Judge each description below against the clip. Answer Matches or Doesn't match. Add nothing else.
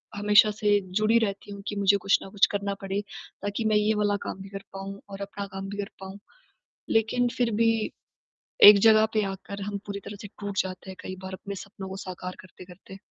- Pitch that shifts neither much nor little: Doesn't match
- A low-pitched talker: Doesn't match